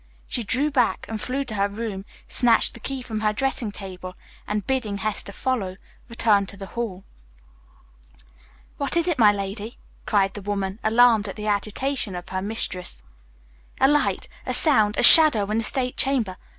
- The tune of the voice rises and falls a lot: No, average, 3.9 semitones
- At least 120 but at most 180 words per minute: Yes, average, 175 wpm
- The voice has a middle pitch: No, high, 215 Hz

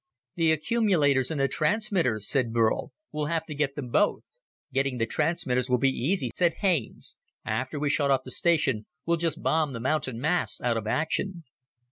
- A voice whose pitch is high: No, medium, 145 Hz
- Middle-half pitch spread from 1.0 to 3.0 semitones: No, average, 4.6 semitones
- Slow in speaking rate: No, average, 180 wpm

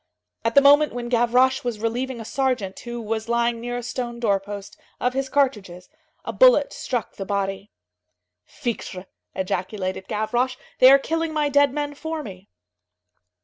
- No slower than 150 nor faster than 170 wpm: Yes, average, 160 wpm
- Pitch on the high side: Yes, high, 240 Hz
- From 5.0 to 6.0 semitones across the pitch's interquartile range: No, average, 4.4 semitones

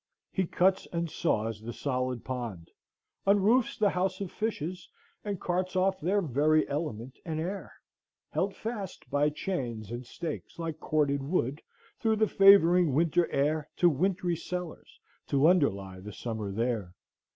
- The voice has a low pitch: No, medium, 160 Hz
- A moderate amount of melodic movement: No, wide, 6.5 semitones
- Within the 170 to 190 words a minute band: No, average, 145 wpm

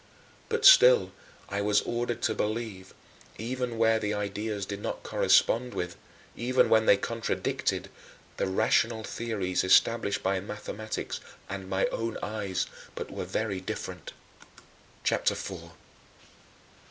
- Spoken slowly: Yes, slow, 130 wpm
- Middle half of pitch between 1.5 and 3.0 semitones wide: Yes, average, 2.7 semitones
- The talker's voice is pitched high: No, low, 110 Hz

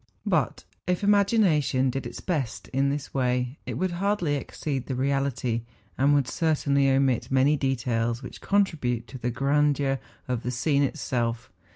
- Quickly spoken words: No, average, 160 wpm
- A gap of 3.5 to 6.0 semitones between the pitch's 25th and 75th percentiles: No, average, 2.9 semitones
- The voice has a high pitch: No, low, 135 Hz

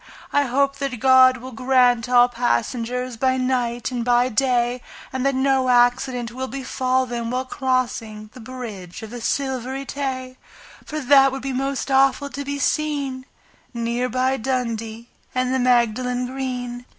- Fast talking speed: No, average, 155 wpm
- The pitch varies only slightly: Yes, narrow, 1.5 semitones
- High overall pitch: Yes, very high, 255 Hz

